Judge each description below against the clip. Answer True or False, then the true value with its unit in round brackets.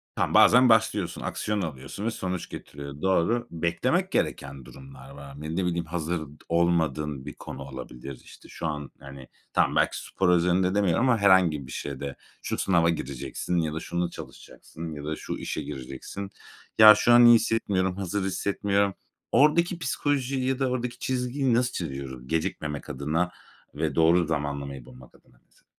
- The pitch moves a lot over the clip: True (6.1 semitones)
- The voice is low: True (85 Hz)